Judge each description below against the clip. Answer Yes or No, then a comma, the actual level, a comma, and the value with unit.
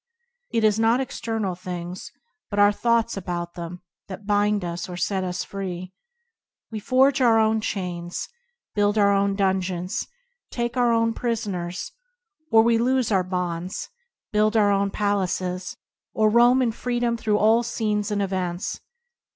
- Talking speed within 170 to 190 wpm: No, average, 145 wpm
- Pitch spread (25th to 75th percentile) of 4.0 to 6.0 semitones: No, average, 3.6 semitones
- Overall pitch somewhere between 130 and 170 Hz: No, high, 205 Hz